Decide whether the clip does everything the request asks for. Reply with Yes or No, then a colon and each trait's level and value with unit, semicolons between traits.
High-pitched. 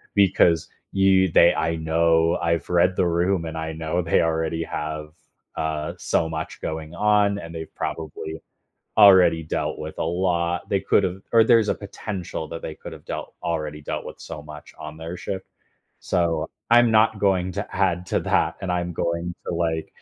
No: very low, 85 Hz